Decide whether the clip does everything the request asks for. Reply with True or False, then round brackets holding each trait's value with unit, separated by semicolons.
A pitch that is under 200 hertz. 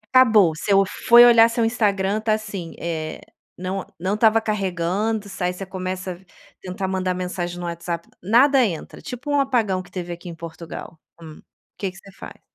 True (190 Hz)